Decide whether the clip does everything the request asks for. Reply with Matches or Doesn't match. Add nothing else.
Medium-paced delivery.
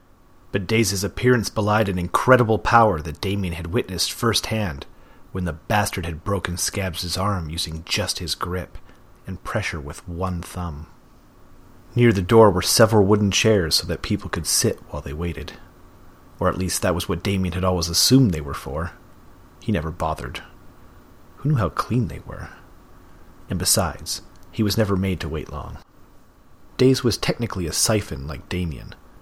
Matches